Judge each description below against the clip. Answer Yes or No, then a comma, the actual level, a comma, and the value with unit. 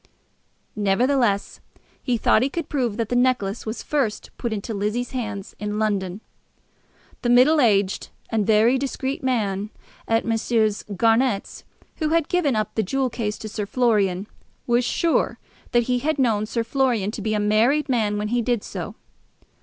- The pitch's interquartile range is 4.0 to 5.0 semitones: No, average, 3.3 semitones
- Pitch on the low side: No, high, 230 Hz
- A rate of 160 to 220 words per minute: Yes, average, 165 wpm